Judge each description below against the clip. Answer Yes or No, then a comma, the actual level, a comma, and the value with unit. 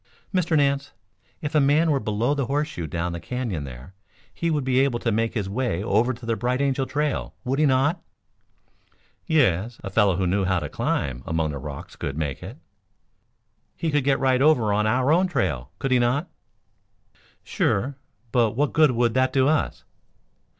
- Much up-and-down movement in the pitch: Yes, wide, 6.3 semitones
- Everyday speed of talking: Yes, average, 185 wpm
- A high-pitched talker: No, low, 125 Hz